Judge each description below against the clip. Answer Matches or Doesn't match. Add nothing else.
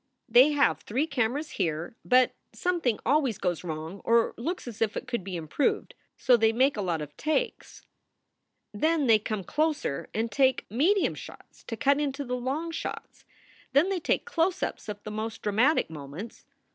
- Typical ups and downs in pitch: Doesn't match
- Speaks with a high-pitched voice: Matches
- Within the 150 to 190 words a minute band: Matches